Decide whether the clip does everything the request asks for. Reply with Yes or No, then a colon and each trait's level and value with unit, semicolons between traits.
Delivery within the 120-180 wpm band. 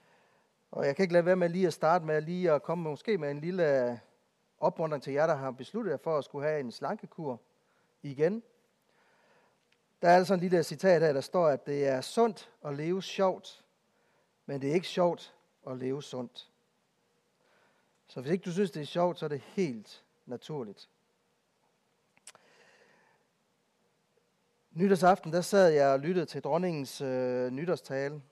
Yes: average, 170 wpm